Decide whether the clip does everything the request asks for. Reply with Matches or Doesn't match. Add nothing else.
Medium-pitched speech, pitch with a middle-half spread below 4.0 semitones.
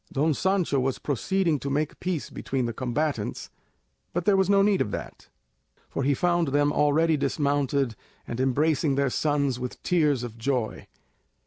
Matches